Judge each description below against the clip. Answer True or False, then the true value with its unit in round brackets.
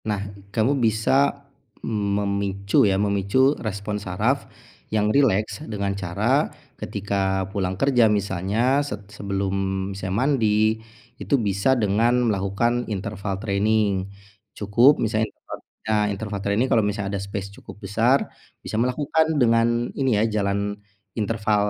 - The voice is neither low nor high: False (105 Hz)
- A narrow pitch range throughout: True (2.2 semitones)